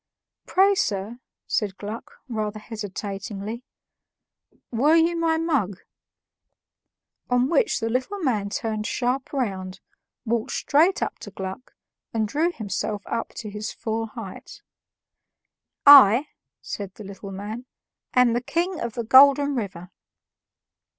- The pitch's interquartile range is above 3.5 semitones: Yes, average, 5.2 semitones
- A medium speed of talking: No, slow, 125 wpm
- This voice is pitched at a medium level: No, high, 230 Hz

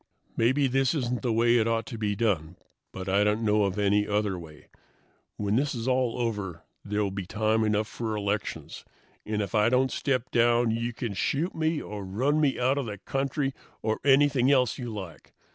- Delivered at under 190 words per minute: No, average, 195 wpm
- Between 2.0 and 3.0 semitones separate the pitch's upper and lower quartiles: No, average, 3.7 semitones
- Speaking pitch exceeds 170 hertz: No, low, 115 Hz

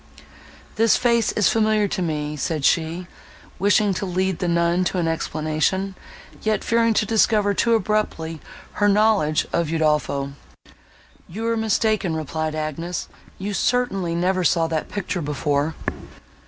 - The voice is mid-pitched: Yes, medium, 180 Hz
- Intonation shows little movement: No, average, 4.9 semitones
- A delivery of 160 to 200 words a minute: No, average, 140 wpm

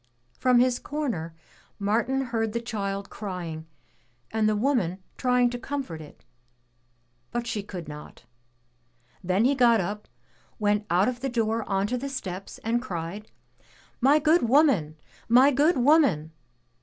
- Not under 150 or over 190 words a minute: No, average, 140 wpm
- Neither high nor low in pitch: No, high, 225 Hz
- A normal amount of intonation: Yes, average, 4.7 semitones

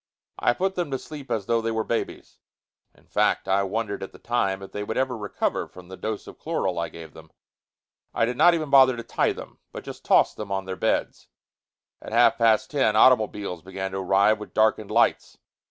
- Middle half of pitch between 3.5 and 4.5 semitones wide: Yes, average, 4.0 semitones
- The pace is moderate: No, fast, 215 wpm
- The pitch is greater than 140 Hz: No, low, 110 Hz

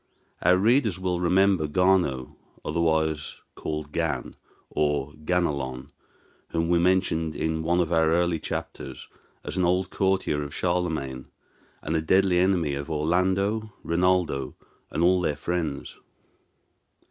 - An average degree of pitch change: Yes, average, 3.1 semitones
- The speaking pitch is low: Yes, very low, 85 Hz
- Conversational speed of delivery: No, slow, 125 wpm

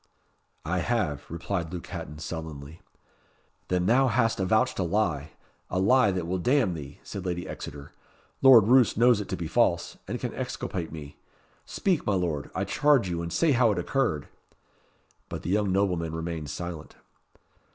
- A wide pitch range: Yes, wide, 5.7 semitones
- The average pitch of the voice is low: Yes, very low, 90 Hz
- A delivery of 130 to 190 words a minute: Yes, average, 165 wpm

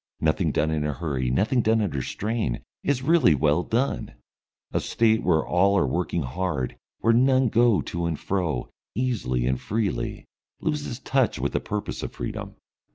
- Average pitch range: No, wide, 7.7 semitones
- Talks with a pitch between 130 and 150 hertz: No, very low, 95 Hz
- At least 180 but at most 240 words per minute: No, average, 165 wpm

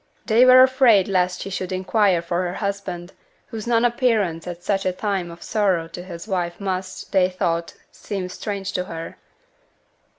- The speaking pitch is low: No, medium, 185 Hz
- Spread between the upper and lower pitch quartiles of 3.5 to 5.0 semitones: No, average, 2.9 semitones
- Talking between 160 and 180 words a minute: Yes, average, 170 wpm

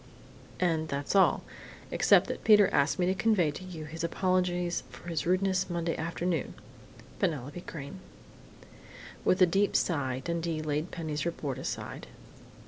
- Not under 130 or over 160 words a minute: Yes, average, 140 wpm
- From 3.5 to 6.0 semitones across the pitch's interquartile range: No, average, 3.0 semitones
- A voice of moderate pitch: Yes, medium, 170 Hz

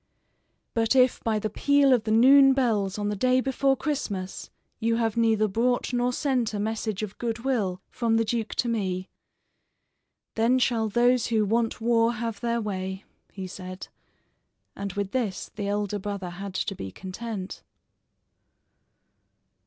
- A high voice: Yes, high, 225 Hz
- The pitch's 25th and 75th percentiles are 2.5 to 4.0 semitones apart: Yes, average, 3.1 semitones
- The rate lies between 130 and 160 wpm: Yes, average, 155 wpm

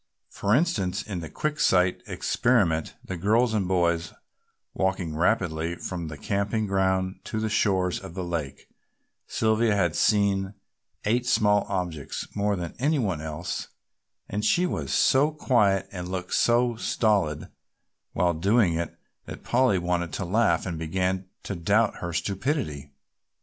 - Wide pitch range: No, average, 4.0 semitones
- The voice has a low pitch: Yes, very low, 95 Hz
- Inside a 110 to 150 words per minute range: Yes, average, 145 wpm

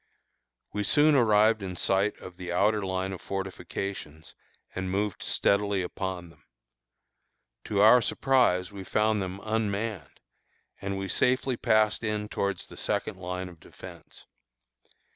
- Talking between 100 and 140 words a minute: Yes, slow, 135 wpm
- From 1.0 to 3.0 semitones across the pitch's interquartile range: Yes, narrow, 2.5 semitones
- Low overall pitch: Yes, low, 100 Hz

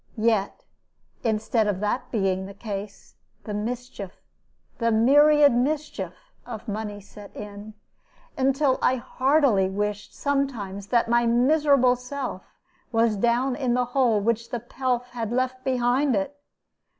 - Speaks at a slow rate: Yes, slow, 130 wpm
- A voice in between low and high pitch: No, high, 235 Hz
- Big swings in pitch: No, average, 3.8 semitones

